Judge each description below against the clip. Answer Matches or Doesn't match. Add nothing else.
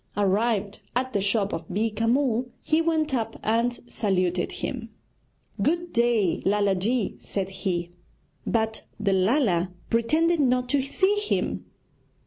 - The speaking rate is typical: Doesn't match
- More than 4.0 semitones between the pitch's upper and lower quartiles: Matches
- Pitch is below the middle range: Doesn't match